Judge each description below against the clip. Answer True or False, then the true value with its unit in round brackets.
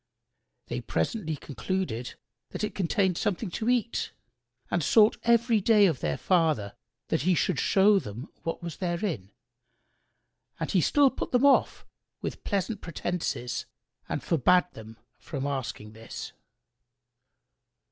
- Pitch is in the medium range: True (180 Hz)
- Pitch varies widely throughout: True (6.9 semitones)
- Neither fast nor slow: False (130 wpm)